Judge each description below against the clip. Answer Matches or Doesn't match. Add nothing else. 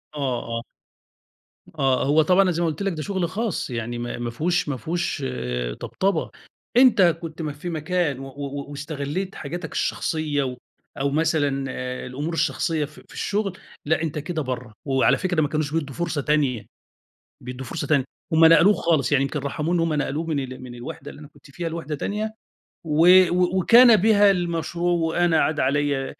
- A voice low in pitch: Doesn't match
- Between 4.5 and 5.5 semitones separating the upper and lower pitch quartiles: Doesn't match